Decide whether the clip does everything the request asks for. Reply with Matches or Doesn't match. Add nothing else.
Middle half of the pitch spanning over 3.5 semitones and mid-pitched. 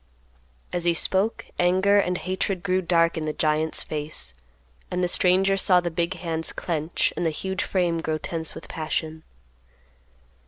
Doesn't match